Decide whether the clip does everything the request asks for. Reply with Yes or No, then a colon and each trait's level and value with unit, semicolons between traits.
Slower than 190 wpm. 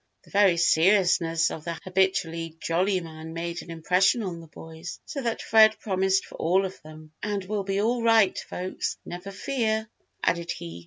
Yes: average, 175 wpm